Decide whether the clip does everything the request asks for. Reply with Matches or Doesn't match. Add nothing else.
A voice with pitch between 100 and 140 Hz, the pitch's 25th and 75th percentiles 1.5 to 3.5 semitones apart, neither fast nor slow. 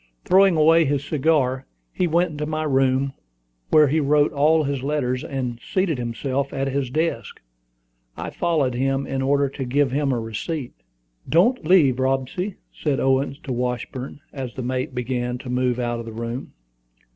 Matches